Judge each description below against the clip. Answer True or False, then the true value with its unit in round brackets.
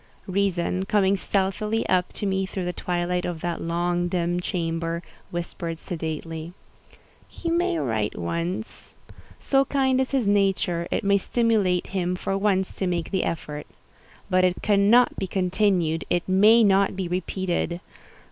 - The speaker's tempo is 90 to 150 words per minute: True (140 wpm)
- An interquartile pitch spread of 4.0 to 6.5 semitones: False (2.6 semitones)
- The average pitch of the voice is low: False (185 Hz)